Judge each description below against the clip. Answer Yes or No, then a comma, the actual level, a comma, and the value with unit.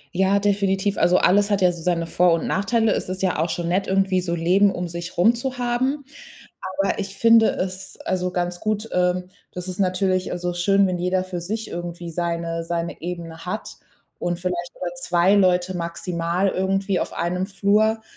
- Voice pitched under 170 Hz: No, medium, 185 Hz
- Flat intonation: Yes, narrow, 2.1 semitones